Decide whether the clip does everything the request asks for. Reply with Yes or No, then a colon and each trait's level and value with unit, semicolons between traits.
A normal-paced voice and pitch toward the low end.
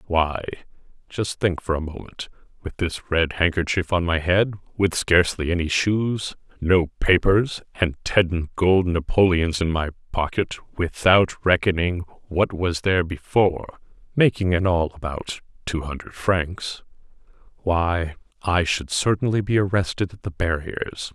No: slow, 130 wpm; very low, 90 Hz